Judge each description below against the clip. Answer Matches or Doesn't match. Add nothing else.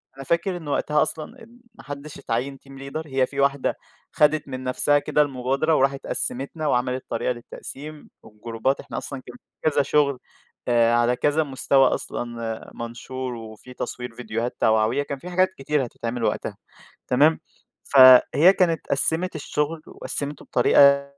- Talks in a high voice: Doesn't match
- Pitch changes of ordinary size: Matches